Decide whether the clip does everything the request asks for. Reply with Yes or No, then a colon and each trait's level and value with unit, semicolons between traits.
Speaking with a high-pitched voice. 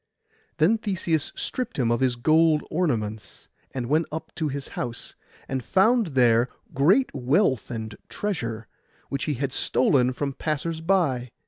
No: medium, 140 Hz